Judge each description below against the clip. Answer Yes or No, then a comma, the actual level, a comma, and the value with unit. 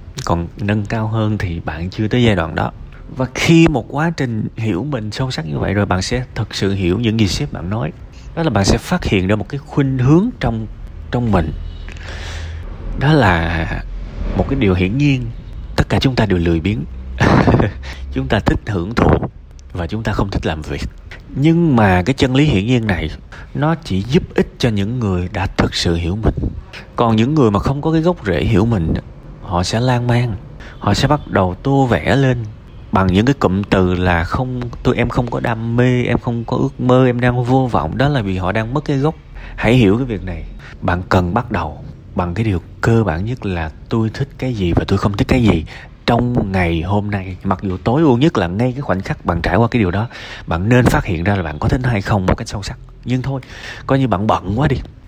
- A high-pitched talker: No, low, 110 Hz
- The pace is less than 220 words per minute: No, average, 235 wpm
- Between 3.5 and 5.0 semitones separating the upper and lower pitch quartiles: No, wide, 5.6 semitones